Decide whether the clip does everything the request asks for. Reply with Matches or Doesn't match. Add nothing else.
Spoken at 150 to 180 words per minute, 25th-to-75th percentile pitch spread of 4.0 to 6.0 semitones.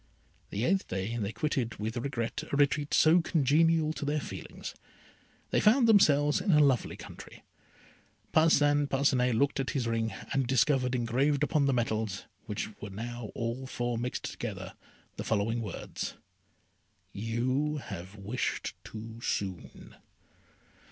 Doesn't match